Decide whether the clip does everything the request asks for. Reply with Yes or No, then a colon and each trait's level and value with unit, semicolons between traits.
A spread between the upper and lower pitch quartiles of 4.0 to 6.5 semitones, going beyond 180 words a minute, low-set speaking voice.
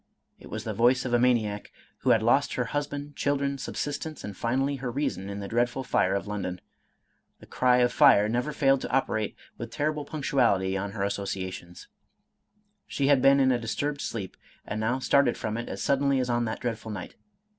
Yes: average, 4.7 semitones; average, 195 wpm; low, 120 Hz